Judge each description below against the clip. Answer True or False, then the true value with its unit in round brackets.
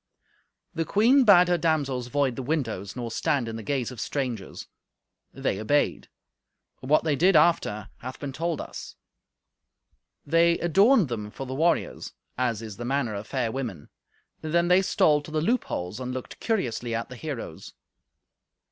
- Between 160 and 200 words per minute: True (165 wpm)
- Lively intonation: True (5.8 semitones)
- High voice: False (135 Hz)